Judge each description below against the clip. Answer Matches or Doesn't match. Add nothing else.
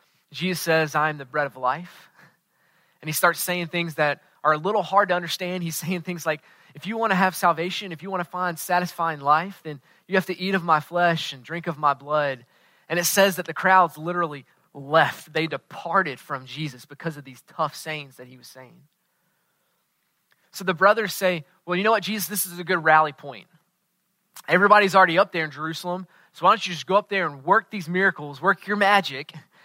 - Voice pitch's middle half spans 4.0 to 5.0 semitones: Doesn't match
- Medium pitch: Matches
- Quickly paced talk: Matches